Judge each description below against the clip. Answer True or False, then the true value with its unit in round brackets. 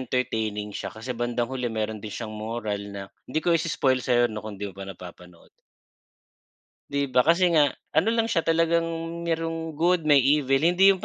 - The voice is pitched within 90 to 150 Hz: True (140 Hz)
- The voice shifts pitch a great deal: True (7.0 semitones)